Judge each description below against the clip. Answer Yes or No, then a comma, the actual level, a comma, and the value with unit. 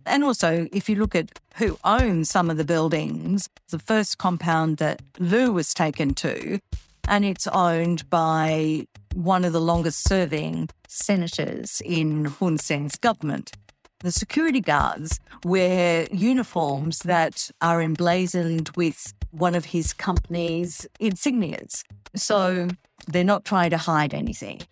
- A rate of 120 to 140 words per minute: Yes, slow, 135 wpm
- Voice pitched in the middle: Yes, medium, 170 Hz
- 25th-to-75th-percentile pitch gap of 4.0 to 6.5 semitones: No, average, 2.9 semitones